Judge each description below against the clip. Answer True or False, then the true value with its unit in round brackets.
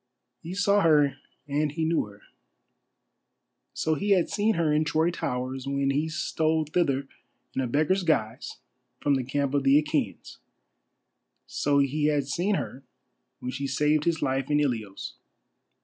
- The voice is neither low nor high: True (145 Hz)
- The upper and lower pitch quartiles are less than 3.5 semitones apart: True (2.9 semitones)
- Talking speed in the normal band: True (155 wpm)